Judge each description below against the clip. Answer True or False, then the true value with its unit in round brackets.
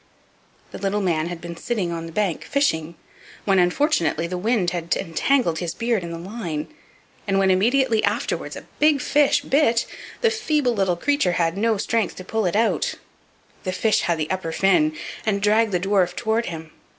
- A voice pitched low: False (195 Hz)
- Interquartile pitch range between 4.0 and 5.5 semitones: True (5.1 semitones)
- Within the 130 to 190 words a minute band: True (185 wpm)